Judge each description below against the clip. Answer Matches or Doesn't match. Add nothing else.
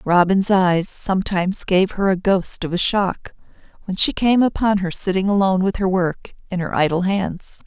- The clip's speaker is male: Doesn't match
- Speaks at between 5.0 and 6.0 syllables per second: Doesn't match